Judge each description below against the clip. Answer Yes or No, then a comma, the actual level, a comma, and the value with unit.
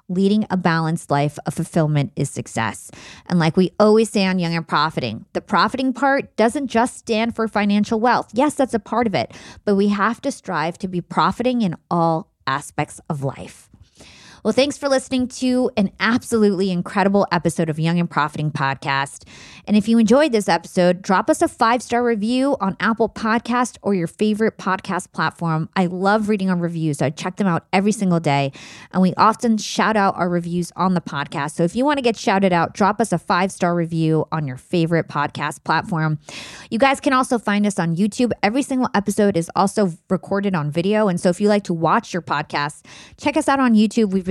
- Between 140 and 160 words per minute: No, average, 200 wpm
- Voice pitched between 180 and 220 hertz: Yes, high, 190 Hz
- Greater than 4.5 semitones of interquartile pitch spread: Yes, average, 5.1 semitones